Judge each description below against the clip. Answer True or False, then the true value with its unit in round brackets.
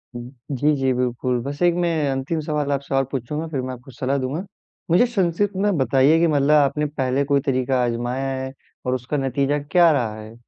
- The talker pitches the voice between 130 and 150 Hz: True (135 Hz)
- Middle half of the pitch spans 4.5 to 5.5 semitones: False (2.8 semitones)